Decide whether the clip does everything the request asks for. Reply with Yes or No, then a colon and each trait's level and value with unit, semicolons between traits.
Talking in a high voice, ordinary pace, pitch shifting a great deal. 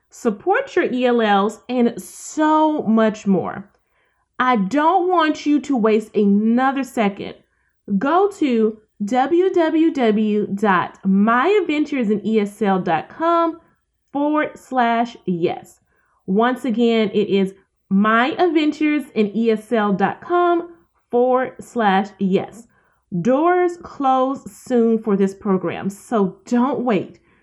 No: high, 235 Hz; slow, 85 wpm; wide, 6.4 semitones